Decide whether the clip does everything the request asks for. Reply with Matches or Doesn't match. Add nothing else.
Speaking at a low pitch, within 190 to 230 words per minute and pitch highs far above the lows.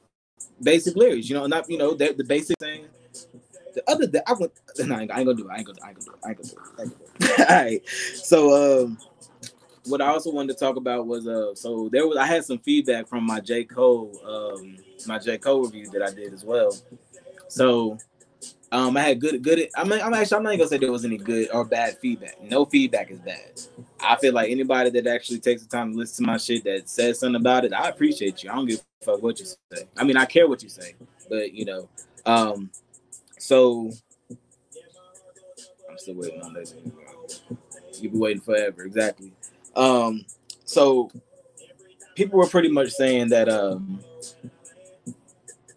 Matches